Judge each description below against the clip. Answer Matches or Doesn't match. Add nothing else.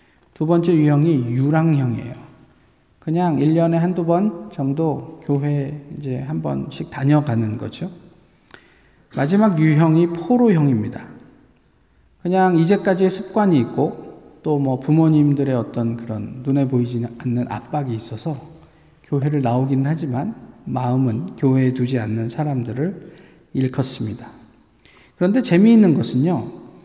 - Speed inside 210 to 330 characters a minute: Matches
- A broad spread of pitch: Doesn't match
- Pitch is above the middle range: Doesn't match